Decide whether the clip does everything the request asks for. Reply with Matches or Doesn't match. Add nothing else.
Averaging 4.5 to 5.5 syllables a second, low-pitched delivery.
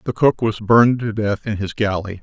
Matches